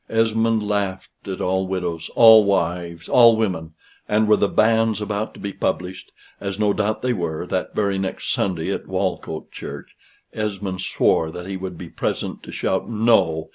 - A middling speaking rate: Yes, average, 175 wpm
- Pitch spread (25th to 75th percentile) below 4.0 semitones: Yes, average, 3.1 semitones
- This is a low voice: Yes, low, 100 Hz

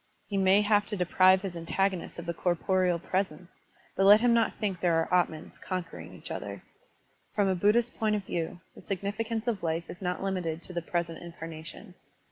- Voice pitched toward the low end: No, medium, 185 Hz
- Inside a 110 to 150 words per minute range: No, average, 195 wpm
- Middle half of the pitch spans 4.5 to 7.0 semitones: No, average, 3.0 semitones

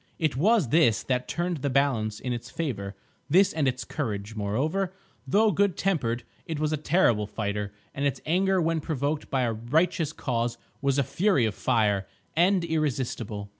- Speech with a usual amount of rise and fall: No, wide, 6.2 semitones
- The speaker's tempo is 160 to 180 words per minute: Yes, average, 170 wpm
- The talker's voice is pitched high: No, medium, 140 Hz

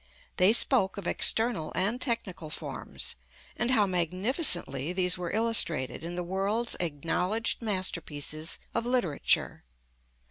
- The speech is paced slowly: Yes, slow, 115 wpm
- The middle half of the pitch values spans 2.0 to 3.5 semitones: No, average, 5.2 semitones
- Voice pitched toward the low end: No, medium, 185 Hz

